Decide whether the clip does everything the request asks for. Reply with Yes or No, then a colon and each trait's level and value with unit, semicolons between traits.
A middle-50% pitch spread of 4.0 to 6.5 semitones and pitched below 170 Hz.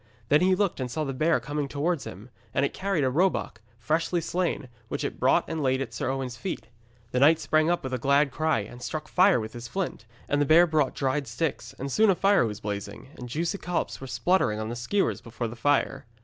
Yes: average, 5.2 semitones; medium, 140 Hz